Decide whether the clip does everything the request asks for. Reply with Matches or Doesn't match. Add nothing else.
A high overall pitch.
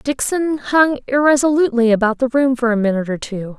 Matches